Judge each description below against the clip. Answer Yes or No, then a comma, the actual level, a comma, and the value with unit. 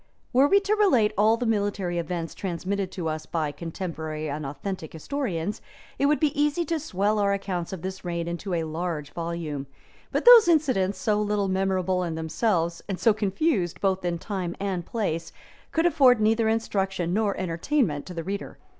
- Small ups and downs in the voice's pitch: No, average, 4.6 semitones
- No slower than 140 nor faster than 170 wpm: No, average, 180 wpm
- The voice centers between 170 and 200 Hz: Yes, high, 190 Hz